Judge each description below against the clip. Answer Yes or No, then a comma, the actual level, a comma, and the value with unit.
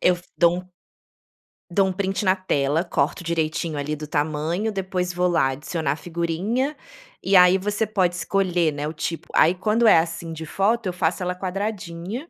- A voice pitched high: No, medium, 180 Hz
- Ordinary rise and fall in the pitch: Yes, average, 3.0 semitones